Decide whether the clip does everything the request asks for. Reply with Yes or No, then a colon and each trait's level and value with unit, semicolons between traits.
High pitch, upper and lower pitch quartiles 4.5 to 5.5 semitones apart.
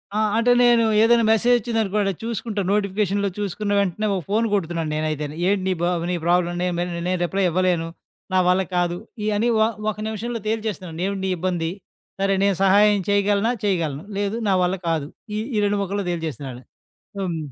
No: high, 195 Hz; average, 3.3 semitones